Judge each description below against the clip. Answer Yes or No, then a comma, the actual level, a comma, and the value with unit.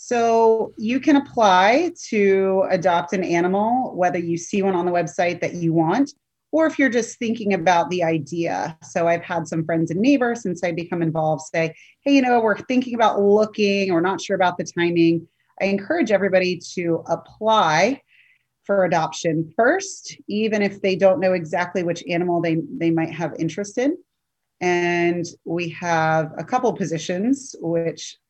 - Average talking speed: Yes, average, 170 wpm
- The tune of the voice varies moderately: Yes, average, 4.6 semitones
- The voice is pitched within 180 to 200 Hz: Yes, medium, 185 Hz